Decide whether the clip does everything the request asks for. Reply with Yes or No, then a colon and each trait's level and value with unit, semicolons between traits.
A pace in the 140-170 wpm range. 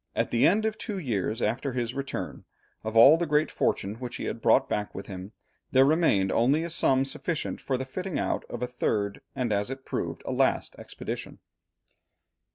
No: average, 195 wpm